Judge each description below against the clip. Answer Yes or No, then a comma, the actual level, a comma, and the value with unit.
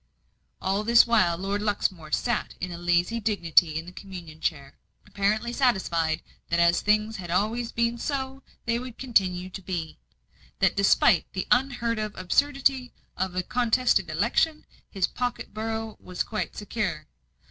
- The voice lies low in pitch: No, high, 210 Hz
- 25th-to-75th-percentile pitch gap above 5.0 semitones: No, average, 4.7 semitones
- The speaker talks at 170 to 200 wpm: No, average, 145 wpm